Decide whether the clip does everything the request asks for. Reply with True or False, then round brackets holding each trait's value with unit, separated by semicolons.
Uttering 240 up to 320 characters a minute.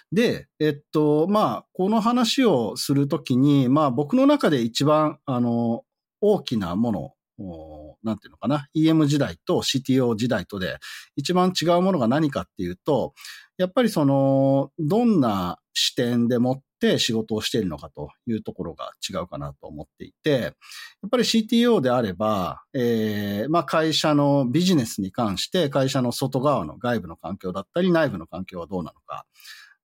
True (310 characters per minute)